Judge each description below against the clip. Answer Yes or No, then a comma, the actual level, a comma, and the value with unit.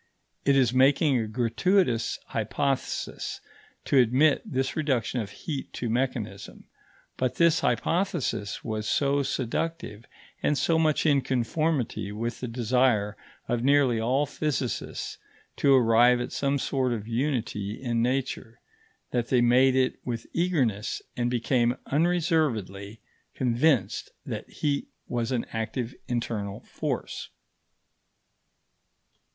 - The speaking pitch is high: No, low, 125 Hz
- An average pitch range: Yes, average, 3.5 semitones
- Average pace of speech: No, slow, 120 wpm